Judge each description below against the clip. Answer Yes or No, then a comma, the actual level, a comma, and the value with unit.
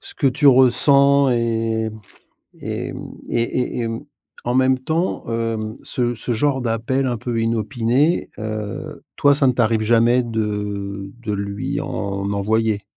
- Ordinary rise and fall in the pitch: Yes, average, 3.0 semitones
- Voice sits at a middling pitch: No, low, 115 Hz